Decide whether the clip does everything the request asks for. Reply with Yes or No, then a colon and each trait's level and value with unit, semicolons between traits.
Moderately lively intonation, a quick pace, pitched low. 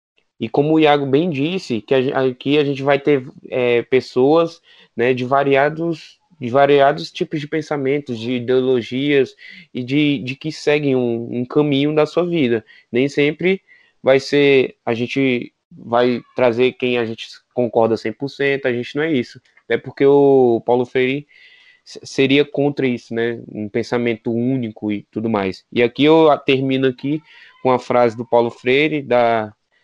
No: average, 3.1 semitones; average, 165 wpm; low, 130 Hz